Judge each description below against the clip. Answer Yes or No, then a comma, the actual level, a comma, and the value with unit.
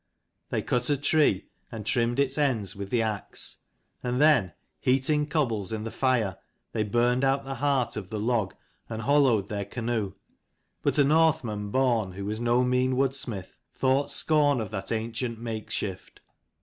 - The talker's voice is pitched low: Yes, low, 120 Hz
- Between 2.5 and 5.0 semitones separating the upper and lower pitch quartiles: Yes, average, 4.0 semitones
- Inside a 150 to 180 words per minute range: Yes, average, 160 wpm